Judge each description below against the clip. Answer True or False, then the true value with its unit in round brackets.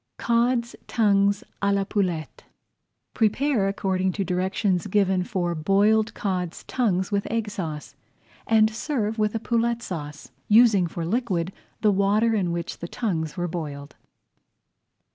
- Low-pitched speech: False (200 Hz)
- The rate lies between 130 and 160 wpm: True (135 wpm)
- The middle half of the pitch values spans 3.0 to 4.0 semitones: True (3.6 semitones)